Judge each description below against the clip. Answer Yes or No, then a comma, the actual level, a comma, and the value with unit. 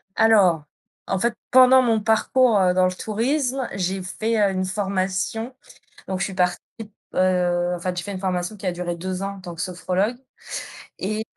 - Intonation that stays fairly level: No, average, 3.4 semitones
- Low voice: No, high, 190 Hz